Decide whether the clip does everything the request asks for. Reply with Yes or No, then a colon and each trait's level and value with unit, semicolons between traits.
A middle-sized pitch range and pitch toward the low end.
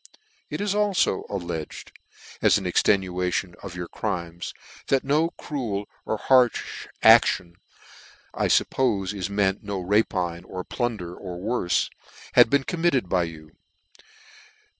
No: wide, 5.7 semitones; low, 100 Hz